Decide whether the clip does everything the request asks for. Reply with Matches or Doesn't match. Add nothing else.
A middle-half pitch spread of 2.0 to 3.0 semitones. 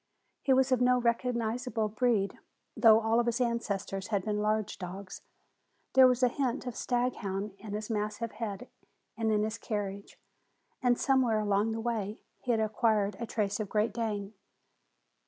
Matches